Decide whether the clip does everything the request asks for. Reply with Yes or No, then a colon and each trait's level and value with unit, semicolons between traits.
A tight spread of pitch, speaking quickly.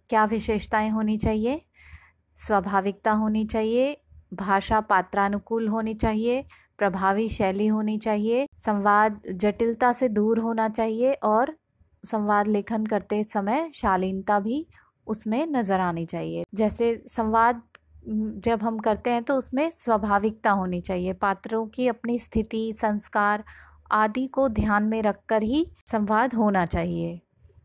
No: narrow, 2.0 semitones; average, 125 wpm